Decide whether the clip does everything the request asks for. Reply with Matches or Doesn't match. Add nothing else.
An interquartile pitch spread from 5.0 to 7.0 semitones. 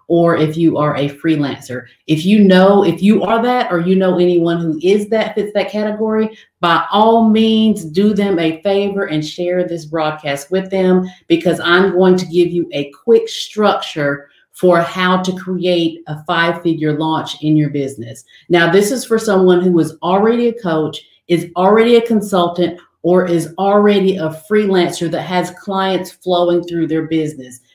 Doesn't match